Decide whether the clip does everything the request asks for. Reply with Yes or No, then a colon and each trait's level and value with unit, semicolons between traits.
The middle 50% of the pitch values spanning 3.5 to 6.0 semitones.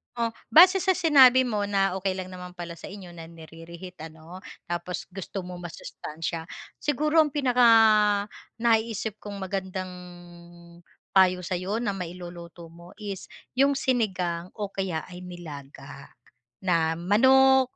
Yes: average, 4.7 semitones